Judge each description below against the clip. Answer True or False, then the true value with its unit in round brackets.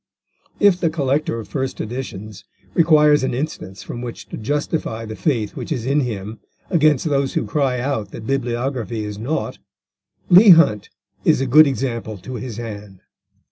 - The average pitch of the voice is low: True (125 Hz)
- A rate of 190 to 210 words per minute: False (165 wpm)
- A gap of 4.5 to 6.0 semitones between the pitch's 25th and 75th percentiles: True (5.1 semitones)